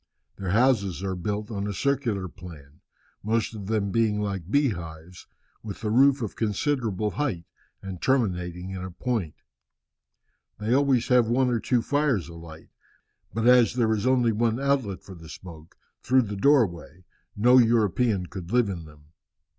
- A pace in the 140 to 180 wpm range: Yes, average, 160 wpm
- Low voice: Yes, low, 105 Hz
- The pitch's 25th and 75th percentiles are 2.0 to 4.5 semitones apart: No, average, 5.2 semitones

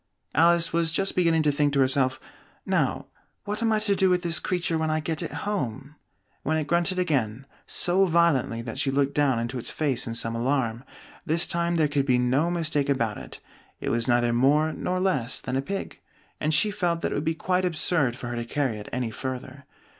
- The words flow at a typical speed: No, fast, 215 wpm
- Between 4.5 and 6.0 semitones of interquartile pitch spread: Yes, average, 4.9 semitones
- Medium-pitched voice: Yes, medium, 150 Hz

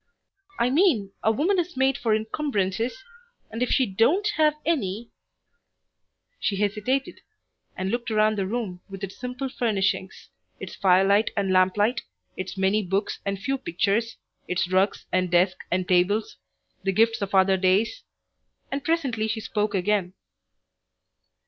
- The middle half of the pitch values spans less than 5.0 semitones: Yes, average, 4.5 semitones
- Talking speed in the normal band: Yes, average, 145 wpm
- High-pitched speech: Yes, high, 210 Hz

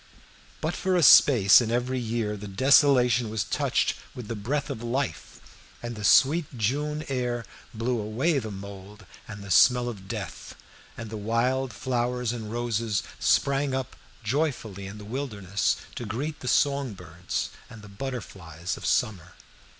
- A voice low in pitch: Yes, low, 120 Hz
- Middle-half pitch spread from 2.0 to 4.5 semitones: Yes, average, 4.0 semitones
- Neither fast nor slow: Yes, average, 160 wpm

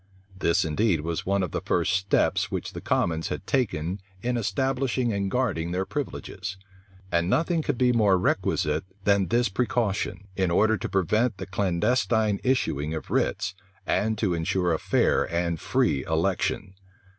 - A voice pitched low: Yes, very low, 95 Hz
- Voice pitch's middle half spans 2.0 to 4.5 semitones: No, average, 5.1 semitones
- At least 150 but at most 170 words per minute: Yes, average, 155 wpm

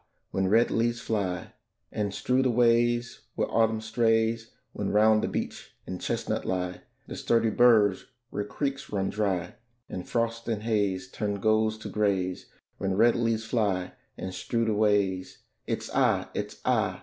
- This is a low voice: Yes, low, 110 Hz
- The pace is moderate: Yes, average, 160 wpm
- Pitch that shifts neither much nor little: Yes, average, 3.0 semitones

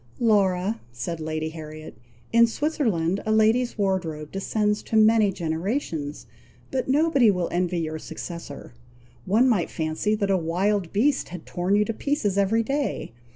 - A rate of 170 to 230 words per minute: No, average, 150 wpm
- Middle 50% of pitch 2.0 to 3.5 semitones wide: No, average, 5.1 semitones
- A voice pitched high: Yes, high, 195 Hz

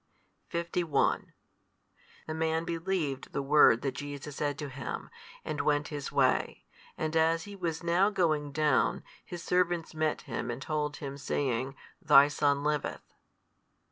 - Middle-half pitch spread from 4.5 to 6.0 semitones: No, narrow, 2.6 semitones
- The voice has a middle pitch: Yes, medium, 150 Hz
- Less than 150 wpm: Yes, average, 140 wpm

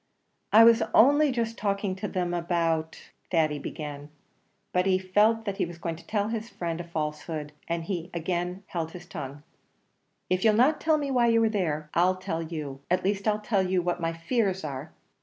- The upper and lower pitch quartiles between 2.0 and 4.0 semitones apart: No, average, 4.5 semitones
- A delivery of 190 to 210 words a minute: Yes, average, 195 wpm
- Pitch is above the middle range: No, medium, 180 Hz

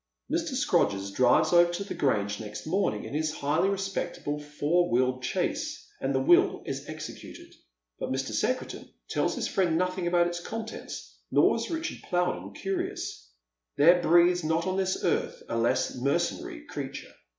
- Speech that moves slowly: No, average, 160 wpm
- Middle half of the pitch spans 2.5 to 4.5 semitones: No, wide, 5.5 semitones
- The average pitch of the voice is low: No, medium, 165 Hz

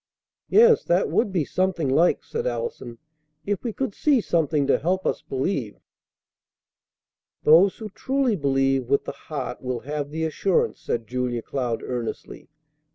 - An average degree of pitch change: No, wide, 7.1 semitones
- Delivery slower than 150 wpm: No, average, 155 wpm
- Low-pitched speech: No, medium, 155 Hz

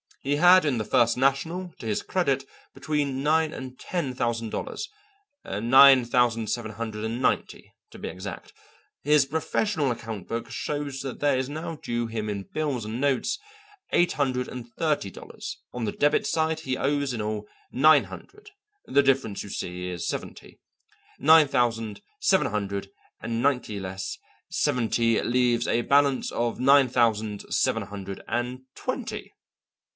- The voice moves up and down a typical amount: Yes, average, 4.3 semitones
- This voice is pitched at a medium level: No, low, 125 Hz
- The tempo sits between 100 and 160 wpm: Yes, average, 155 wpm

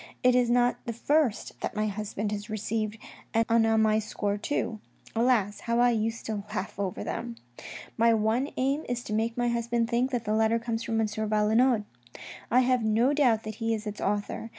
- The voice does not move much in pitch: Yes, narrow, 2.0 semitones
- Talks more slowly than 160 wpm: No, average, 200 wpm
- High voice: Yes, high, 225 Hz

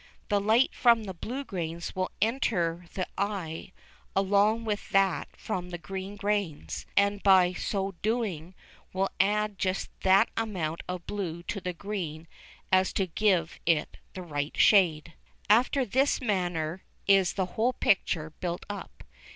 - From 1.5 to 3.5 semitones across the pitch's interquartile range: Yes, average, 3.2 semitones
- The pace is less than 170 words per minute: Yes, average, 145 wpm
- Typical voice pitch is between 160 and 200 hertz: Yes, high, 190 Hz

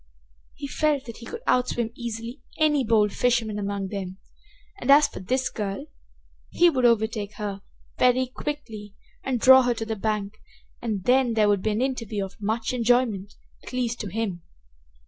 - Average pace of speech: Yes, average, 170 wpm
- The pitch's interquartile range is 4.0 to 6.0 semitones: No, average, 3.4 semitones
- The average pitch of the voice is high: Yes, high, 230 Hz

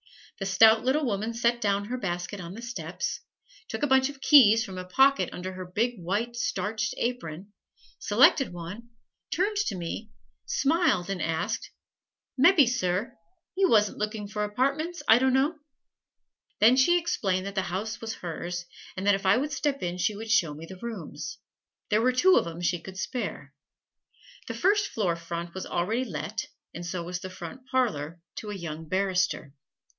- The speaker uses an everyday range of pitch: No, wide, 5.8 semitones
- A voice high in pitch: Yes, high, 210 Hz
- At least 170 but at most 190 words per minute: Yes, average, 175 wpm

